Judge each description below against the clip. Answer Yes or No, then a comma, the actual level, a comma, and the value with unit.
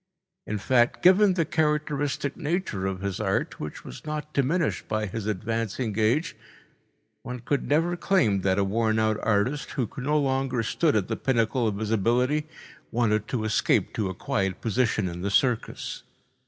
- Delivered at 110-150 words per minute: No, average, 170 wpm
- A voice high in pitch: No, low, 115 Hz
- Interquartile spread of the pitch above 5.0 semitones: Yes, wide, 5.6 semitones